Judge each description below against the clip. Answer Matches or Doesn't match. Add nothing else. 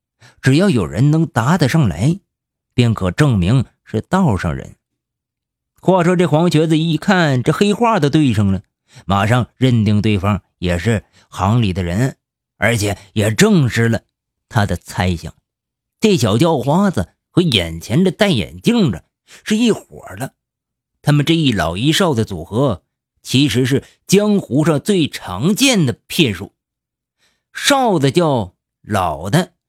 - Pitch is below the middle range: Matches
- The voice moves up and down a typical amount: Doesn't match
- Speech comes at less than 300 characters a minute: Matches